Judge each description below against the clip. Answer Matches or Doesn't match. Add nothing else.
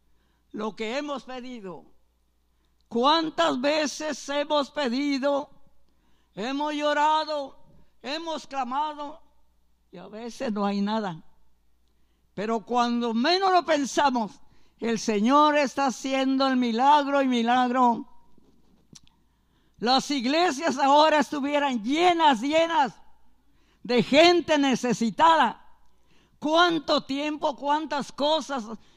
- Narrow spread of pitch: Doesn't match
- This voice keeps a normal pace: Doesn't match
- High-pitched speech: Matches